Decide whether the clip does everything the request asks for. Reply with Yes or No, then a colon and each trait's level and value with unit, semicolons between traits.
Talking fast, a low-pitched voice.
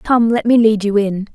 No: fast, 270 wpm; high, 220 Hz